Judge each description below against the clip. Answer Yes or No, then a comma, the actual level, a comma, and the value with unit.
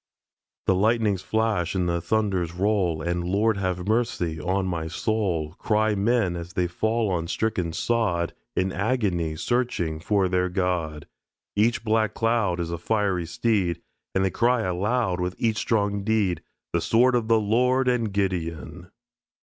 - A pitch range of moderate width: Yes, average, 4.1 semitones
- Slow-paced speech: No, average, 155 wpm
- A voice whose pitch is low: Yes, very low, 95 Hz